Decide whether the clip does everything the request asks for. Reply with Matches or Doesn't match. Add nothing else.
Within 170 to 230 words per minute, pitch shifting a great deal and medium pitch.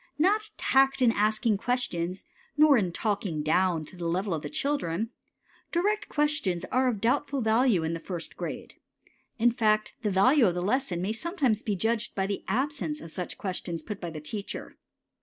Doesn't match